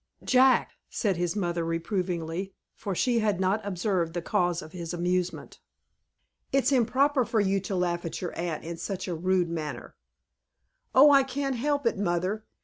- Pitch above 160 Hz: Yes, medium, 185 Hz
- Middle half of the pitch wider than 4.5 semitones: Yes, average, 5.1 semitones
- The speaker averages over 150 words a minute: Yes, average, 165 wpm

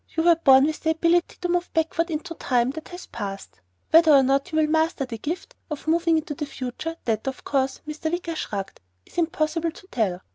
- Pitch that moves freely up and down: No, average, 3.8 semitones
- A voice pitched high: Yes, very high, 315 Hz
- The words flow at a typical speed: No, fast, 220 wpm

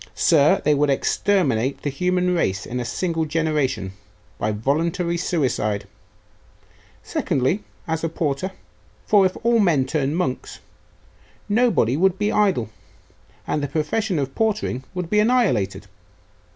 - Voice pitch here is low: No, medium, 160 Hz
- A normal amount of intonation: No, wide, 5.9 semitones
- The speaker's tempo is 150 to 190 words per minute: No, slow, 135 wpm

